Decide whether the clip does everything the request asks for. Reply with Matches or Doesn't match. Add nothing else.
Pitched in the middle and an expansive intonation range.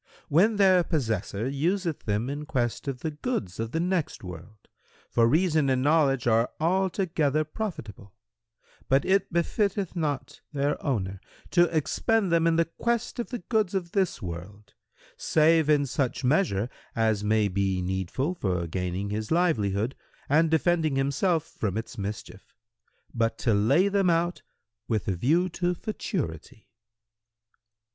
Matches